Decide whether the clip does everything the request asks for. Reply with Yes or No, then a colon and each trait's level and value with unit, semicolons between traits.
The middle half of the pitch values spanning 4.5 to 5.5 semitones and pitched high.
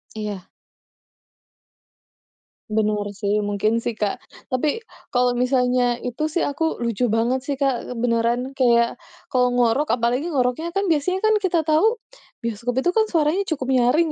Yes: average, 4.8 semitones; very high, 250 Hz